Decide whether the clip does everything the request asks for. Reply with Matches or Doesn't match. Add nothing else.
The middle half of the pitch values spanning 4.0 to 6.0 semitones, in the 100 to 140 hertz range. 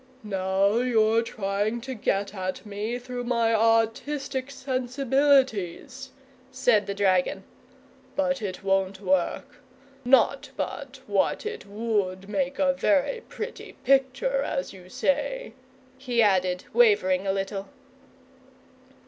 Doesn't match